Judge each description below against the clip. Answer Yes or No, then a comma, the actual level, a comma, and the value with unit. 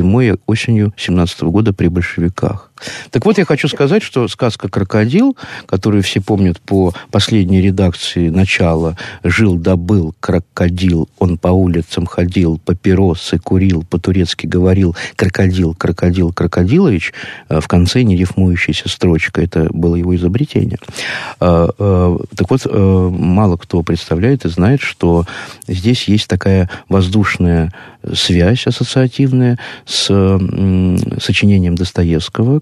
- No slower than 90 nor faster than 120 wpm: Yes, average, 115 wpm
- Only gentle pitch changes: No, average, 3.4 semitones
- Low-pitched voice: Yes, very low, 95 Hz